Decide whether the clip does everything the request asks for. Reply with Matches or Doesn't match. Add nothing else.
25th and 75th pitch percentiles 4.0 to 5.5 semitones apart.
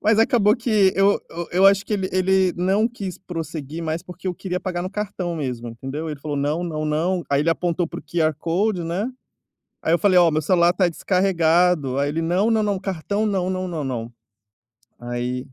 Doesn't match